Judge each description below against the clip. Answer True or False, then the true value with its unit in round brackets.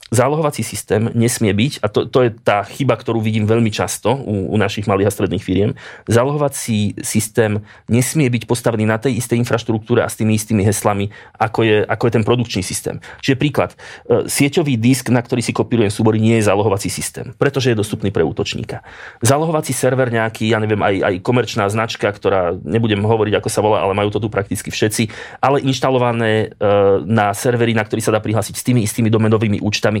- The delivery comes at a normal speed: False (190 wpm)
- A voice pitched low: True (115 Hz)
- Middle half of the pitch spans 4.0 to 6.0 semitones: False (2.6 semitones)